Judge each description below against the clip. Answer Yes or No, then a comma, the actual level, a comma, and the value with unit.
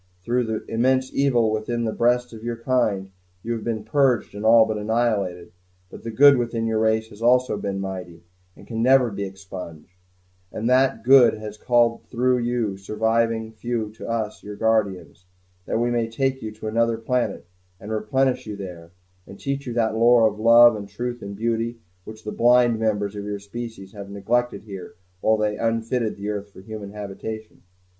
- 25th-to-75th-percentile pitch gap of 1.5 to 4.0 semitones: Yes, narrow, 2.4 semitones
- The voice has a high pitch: No, low, 110 Hz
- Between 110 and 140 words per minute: No, average, 185 wpm